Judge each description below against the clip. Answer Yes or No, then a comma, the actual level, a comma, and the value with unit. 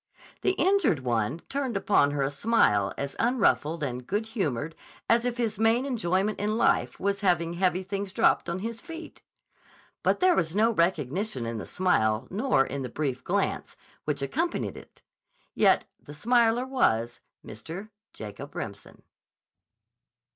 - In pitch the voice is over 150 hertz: Yes, high, 190 Hz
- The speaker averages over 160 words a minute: No, average, 150 wpm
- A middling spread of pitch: No, wide, 8.4 semitones